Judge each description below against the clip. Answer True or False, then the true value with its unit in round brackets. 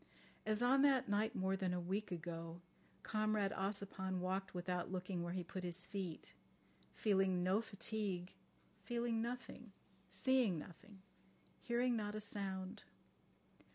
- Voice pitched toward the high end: True (195 Hz)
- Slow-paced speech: True (130 wpm)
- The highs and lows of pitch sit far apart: False (2.9 semitones)